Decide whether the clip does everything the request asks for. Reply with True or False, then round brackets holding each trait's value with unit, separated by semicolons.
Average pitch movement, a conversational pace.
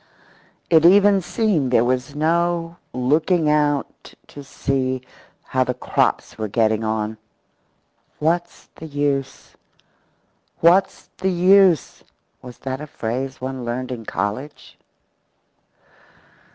False (5.0 semitones; 110 wpm)